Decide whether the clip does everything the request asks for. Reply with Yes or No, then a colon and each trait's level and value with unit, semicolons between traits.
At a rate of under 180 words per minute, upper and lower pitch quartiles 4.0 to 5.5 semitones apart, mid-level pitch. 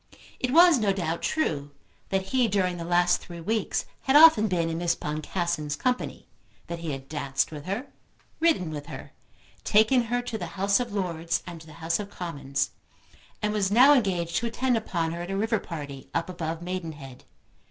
No: average, 190 wpm; average, 5.1 semitones; medium, 180 Hz